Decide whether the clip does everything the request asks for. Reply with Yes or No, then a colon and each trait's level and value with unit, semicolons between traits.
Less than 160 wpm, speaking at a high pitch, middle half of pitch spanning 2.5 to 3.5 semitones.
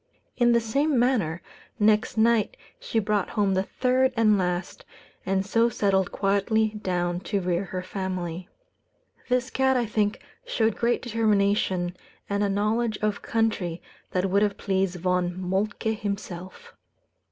Yes: average, 140 wpm; high, 205 Hz; average, 3.2 semitones